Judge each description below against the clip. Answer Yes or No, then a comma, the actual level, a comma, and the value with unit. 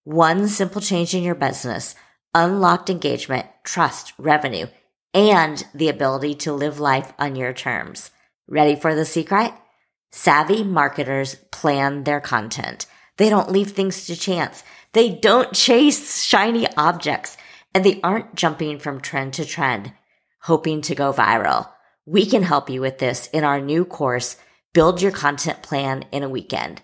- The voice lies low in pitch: No, medium, 155 Hz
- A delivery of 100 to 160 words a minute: Yes, average, 150 wpm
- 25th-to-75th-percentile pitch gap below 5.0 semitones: No, wide, 5.4 semitones